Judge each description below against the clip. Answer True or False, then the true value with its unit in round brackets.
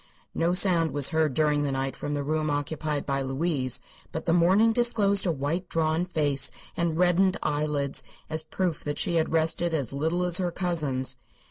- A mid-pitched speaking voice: True (160 Hz)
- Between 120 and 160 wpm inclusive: False (185 wpm)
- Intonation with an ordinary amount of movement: True (3.3 semitones)